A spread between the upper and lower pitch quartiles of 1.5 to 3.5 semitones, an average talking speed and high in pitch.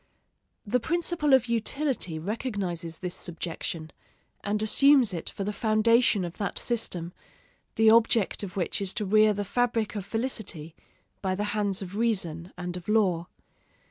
No: average, 4.3 semitones; average, 150 wpm; high, 205 Hz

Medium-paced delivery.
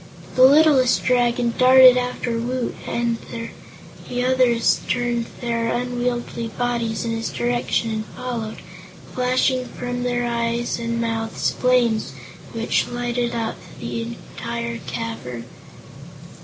No: slow, 115 wpm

